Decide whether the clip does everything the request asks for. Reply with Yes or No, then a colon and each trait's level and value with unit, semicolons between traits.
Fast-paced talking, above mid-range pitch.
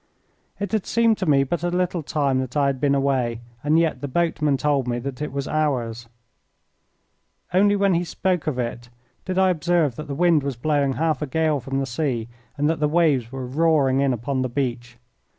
No: fast, 210 wpm; medium, 145 Hz